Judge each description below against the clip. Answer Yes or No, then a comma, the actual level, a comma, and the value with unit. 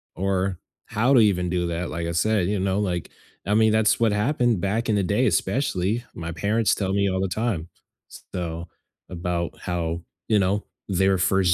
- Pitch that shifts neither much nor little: Yes, average, 3.5 semitones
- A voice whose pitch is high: No, very low, 95 Hz